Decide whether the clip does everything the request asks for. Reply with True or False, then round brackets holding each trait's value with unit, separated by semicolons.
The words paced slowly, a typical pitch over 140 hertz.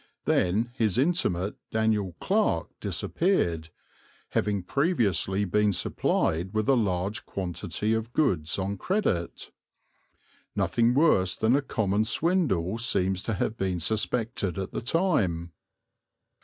False (115 wpm; 105 Hz)